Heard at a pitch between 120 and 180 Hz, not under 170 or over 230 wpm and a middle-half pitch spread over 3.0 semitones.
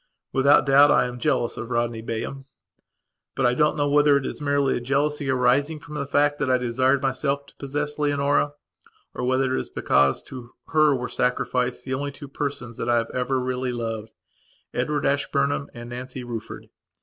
No: low, 135 Hz; average, 185 wpm; narrow, 2.5 semitones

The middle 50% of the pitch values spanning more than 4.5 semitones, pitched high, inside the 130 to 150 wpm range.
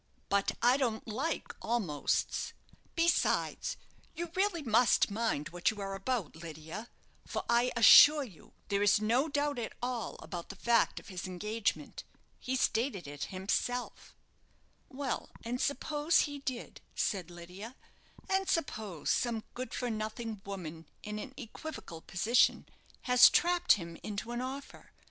Yes: average, 5.0 semitones; high, 230 Hz; average, 140 wpm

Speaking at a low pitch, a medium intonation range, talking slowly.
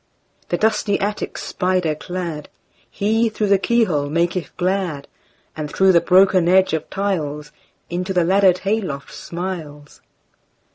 No: medium, 185 Hz; average, 3.6 semitones; slow, 115 wpm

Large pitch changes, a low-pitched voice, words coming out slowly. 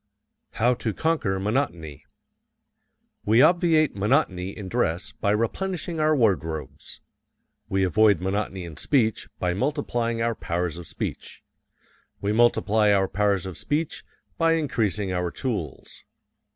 Yes: wide, 5.9 semitones; low, 105 Hz; slow, 125 wpm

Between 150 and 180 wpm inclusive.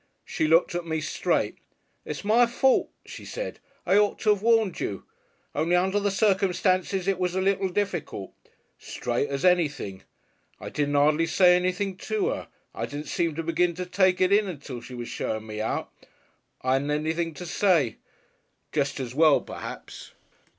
Yes: average, 170 wpm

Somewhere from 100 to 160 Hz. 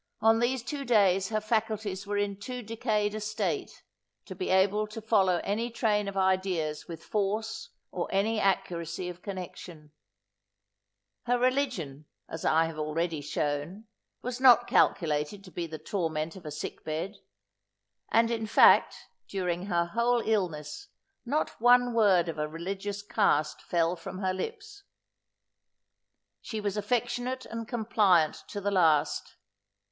No: high, 200 Hz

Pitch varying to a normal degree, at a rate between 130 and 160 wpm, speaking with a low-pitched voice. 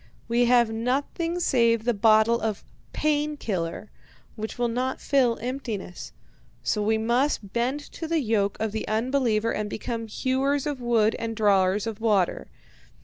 No: average, 3.2 semitones; average, 150 wpm; high, 230 Hz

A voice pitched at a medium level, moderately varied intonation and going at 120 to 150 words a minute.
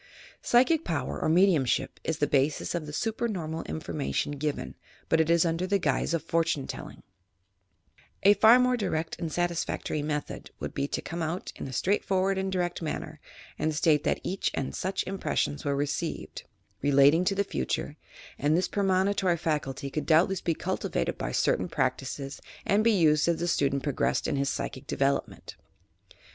No: medium, 165 Hz; average, 4.4 semitones; average, 175 wpm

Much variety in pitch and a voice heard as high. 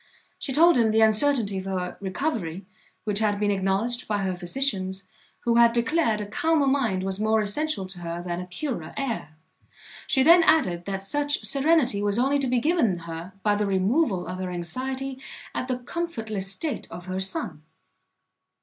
Yes: wide, 6.1 semitones; high, 215 Hz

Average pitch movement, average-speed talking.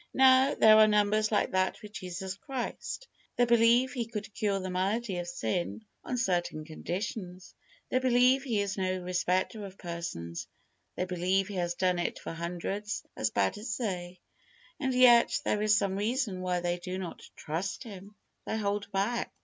Yes: average, 3.8 semitones; average, 175 wpm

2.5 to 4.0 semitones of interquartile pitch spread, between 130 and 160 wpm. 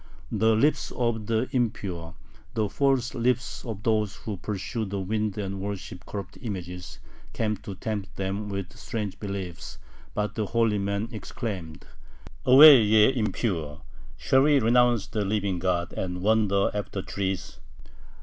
Yes: average, 2.8 semitones; average, 140 wpm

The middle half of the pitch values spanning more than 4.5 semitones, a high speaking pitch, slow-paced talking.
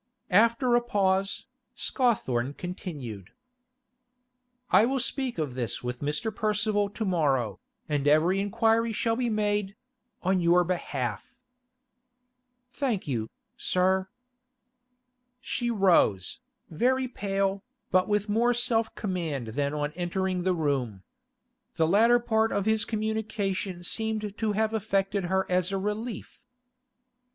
Yes: average, 5.0 semitones; high, 195 Hz; slow, 120 wpm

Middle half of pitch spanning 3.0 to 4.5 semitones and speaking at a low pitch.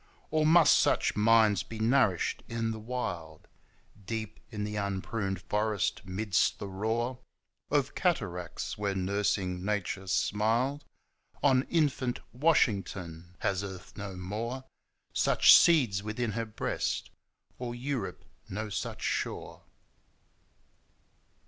Yes: average, 4.1 semitones; low, 105 Hz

